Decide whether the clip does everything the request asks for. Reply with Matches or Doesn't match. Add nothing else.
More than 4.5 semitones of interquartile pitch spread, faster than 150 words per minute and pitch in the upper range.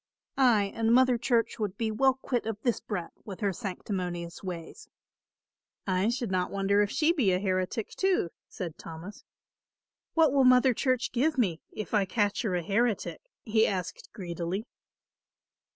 Matches